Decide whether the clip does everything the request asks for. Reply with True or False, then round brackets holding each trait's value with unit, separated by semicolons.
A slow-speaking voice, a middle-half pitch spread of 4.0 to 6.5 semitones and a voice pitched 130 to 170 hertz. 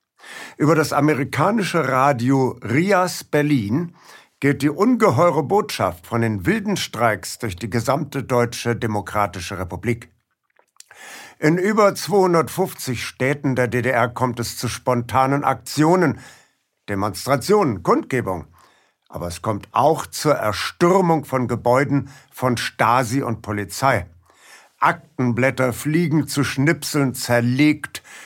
True (105 wpm; 5.2 semitones; 135 Hz)